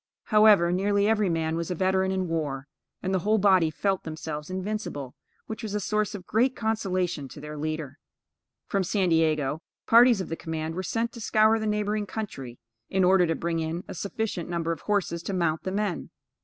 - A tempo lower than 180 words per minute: No, average, 195 wpm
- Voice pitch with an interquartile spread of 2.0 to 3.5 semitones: No, average, 4.4 semitones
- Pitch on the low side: No, medium, 185 Hz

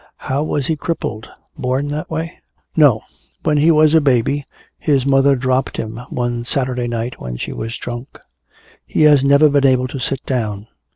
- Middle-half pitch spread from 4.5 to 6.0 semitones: No, average, 3.2 semitones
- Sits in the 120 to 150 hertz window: Yes, low, 135 Hz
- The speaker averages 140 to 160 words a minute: No, average, 175 wpm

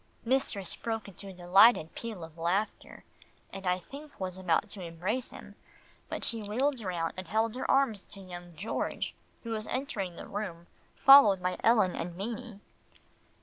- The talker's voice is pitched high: Yes, high, 200 Hz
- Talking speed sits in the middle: Yes, average, 170 wpm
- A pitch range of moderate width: Yes, average, 4.2 semitones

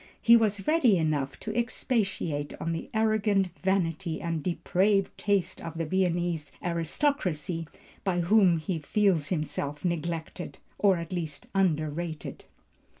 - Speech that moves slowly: Yes, slow, 125 wpm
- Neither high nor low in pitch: Yes, medium, 175 Hz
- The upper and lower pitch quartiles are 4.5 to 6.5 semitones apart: No, average, 3.6 semitones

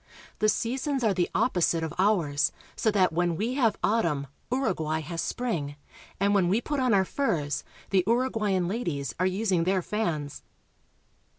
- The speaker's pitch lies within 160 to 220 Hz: Yes, high, 190 Hz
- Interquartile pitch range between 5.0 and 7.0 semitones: Yes, average, 5.3 semitones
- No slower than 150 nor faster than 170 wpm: Yes, average, 165 wpm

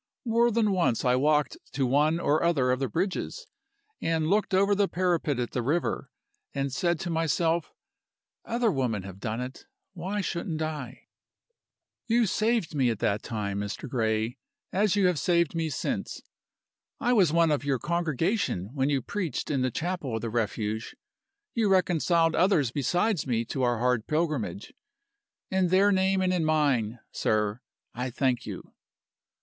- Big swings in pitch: Yes, wide, 6.6 semitones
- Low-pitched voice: No, medium, 155 Hz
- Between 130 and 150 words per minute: No, average, 165 wpm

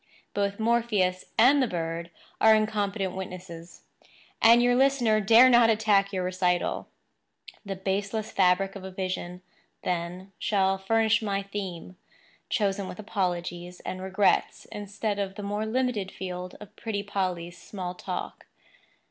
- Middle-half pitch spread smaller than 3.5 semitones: Yes, average, 2.9 semitones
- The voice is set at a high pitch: Yes, high, 195 Hz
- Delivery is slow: Yes, slow, 130 wpm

